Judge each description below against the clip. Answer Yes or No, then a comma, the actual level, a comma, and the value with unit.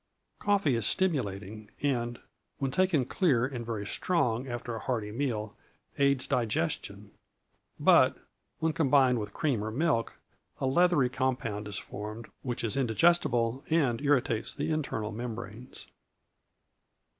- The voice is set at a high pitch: No, low, 125 Hz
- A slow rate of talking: Yes, slow, 125 wpm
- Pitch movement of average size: Yes, average, 4.1 semitones